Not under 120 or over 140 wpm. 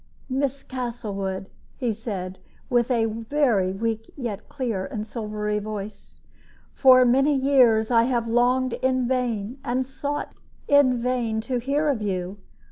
Yes: slow, 135 wpm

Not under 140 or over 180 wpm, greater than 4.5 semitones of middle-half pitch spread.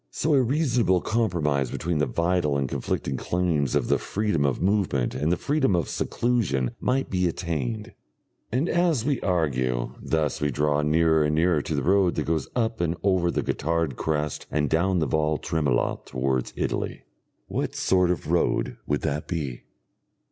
Yes: average, 170 wpm; average, 4.9 semitones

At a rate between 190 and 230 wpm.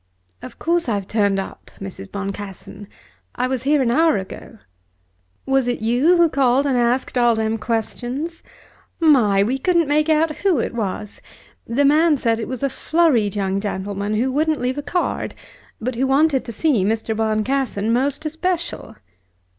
No: average, 165 wpm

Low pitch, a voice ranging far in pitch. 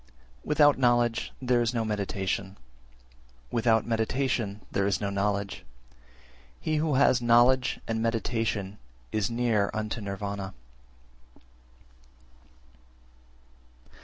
No: low, 115 Hz; average, 3.2 semitones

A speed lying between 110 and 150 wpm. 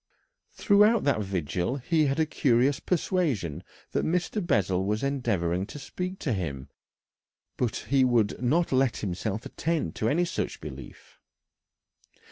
Yes: slow, 135 wpm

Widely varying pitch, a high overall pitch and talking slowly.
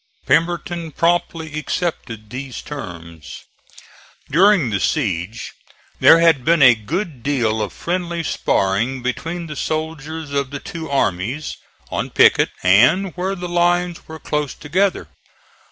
No: wide, 5.7 semitones; medium, 150 Hz; slow, 125 wpm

